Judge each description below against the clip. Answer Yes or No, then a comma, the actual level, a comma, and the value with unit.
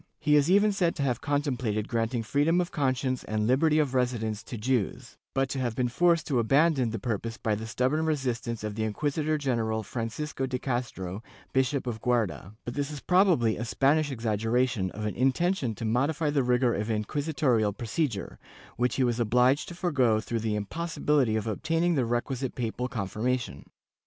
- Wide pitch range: No, average, 4.5 semitones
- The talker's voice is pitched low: Yes, low, 125 Hz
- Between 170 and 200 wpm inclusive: Yes, average, 180 wpm